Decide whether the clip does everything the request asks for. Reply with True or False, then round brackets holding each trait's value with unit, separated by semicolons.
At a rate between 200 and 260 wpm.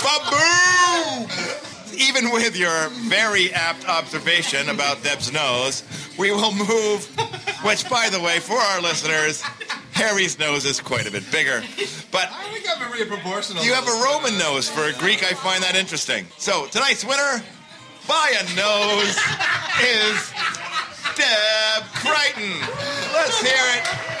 False (140 wpm)